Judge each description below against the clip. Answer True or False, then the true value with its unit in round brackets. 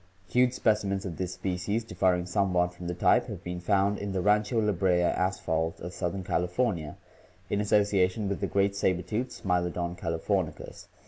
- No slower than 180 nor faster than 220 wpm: True (185 wpm)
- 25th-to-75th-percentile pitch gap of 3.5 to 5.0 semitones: False (2.5 semitones)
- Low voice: True (95 Hz)